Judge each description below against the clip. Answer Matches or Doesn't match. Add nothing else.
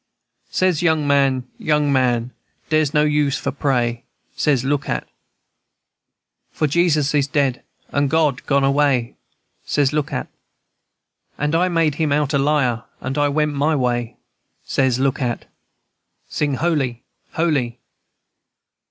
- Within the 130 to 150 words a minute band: Matches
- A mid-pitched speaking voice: Matches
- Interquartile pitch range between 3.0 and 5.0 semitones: Doesn't match